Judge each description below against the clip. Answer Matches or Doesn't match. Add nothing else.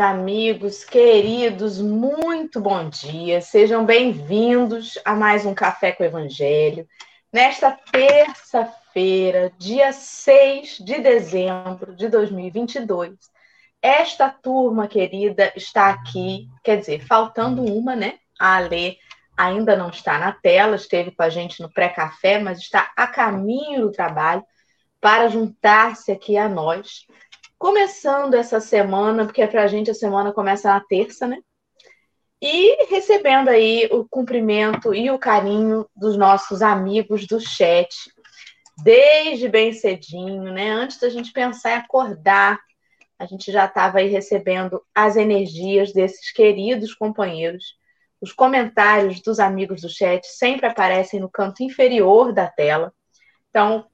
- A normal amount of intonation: Matches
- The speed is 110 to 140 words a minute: Matches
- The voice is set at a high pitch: Matches